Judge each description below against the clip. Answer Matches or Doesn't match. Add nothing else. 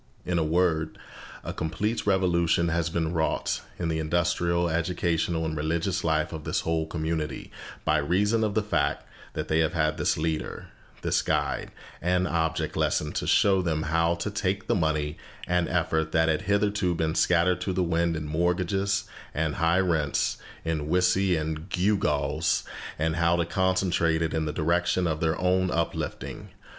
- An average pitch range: Doesn't match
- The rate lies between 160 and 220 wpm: Matches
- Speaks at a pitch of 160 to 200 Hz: Doesn't match